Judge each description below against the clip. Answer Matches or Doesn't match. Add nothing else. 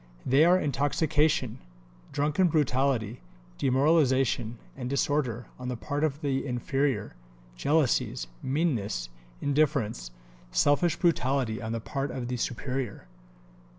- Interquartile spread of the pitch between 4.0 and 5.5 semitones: Doesn't match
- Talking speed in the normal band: Doesn't match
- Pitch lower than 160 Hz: Matches